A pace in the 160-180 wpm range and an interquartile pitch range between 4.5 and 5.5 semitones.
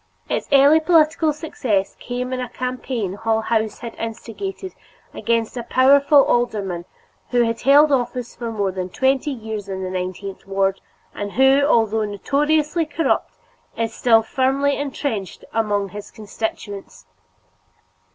No: slow, 135 wpm; average, 5.1 semitones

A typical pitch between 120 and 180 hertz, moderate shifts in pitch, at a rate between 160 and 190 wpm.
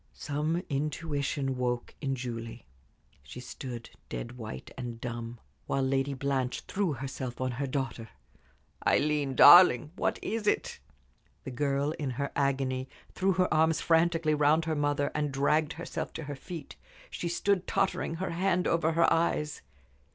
No: medium, 140 Hz; average, 3.9 semitones; average, 150 wpm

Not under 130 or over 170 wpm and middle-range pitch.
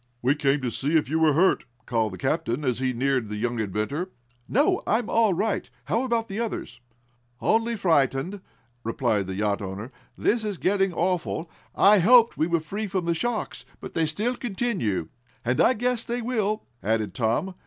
No: average, 185 wpm; medium, 165 Hz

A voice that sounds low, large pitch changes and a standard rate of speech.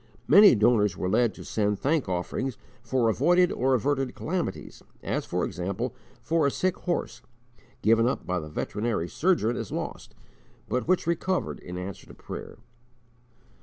Yes: low, 120 Hz; wide, 7.4 semitones; average, 155 wpm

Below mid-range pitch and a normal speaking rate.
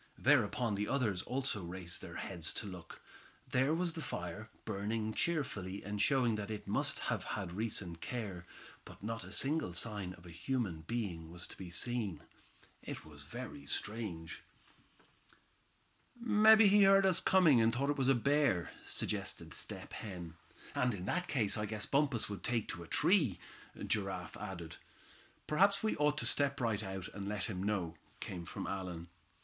Yes: low, 105 Hz; average, 170 wpm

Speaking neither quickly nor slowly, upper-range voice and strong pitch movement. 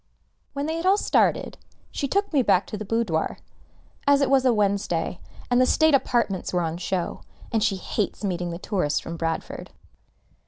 Yes: average, 185 wpm; high, 210 Hz; wide, 7.5 semitones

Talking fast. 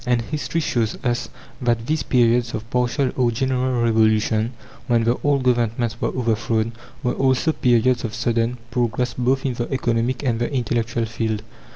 No: average, 165 wpm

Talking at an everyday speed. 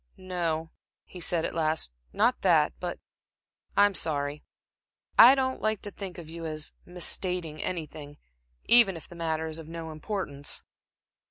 Yes: average, 150 wpm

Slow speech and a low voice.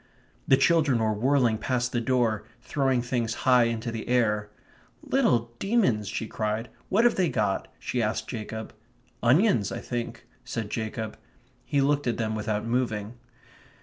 No: average, 150 wpm; low, 120 Hz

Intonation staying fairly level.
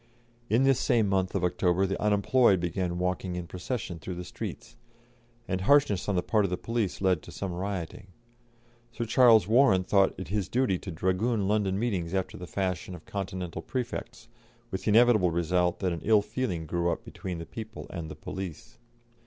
No: average, 3.3 semitones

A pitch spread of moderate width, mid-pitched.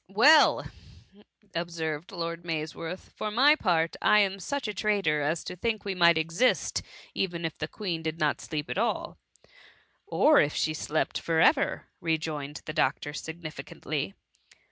Yes: average, 4.0 semitones; medium, 165 Hz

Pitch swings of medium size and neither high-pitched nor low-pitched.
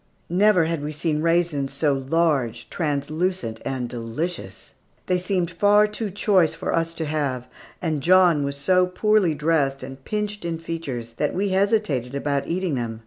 Yes: average, 4.7 semitones; medium, 165 Hz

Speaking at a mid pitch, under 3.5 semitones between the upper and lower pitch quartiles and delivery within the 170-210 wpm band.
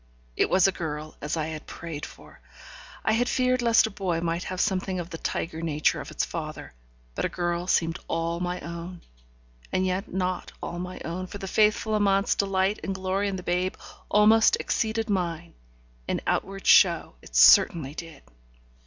Yes: medium, 180 Hz; average, 2.7 semitones; average, 180 wpm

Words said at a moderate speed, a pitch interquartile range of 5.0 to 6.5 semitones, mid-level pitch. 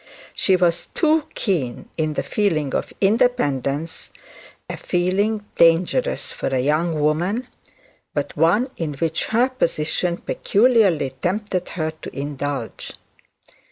No: slow, 120 wpm; wide, 5.4 semitones; medium, 170 Hz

